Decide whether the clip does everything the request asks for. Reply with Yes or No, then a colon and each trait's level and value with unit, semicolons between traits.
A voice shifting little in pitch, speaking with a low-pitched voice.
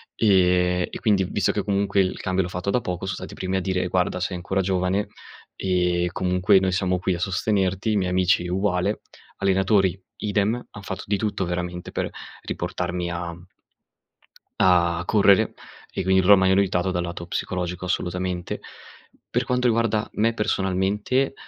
Yes: narrow, 1.8 semitones; very low, 95 Hz